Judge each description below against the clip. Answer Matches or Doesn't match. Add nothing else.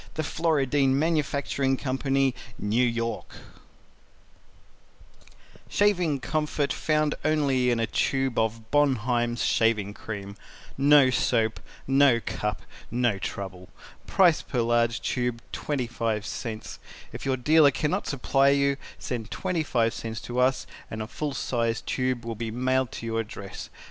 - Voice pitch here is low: Matches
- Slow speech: Matches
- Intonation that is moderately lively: Matches